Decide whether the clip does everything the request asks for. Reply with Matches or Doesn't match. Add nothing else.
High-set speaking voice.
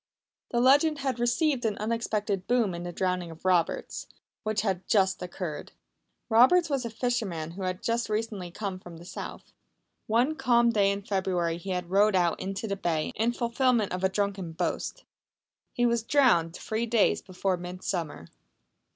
Matches